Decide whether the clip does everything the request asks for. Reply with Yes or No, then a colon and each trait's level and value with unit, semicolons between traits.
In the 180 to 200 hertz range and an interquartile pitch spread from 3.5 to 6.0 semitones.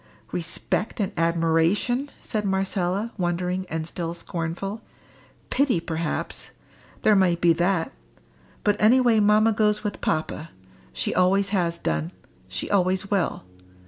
Yes: medium, 185 Hz; average, 3.8 semitones